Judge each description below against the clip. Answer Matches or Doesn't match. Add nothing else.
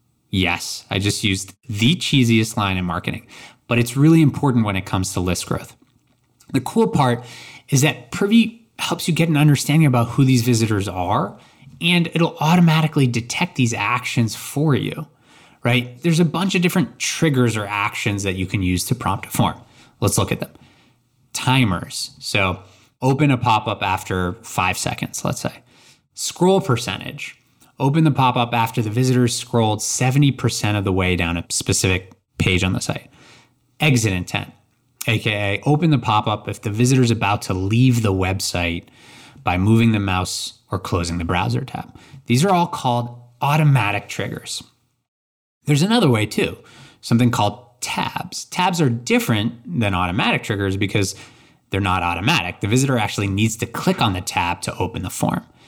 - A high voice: Doesn't match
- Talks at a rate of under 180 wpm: Matches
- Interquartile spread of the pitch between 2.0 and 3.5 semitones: Doesn't match